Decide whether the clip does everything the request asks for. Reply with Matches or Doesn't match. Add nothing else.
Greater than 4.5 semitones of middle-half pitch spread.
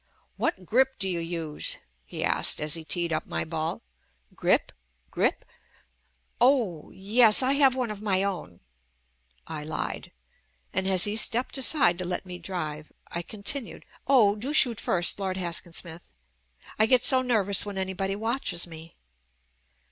Matches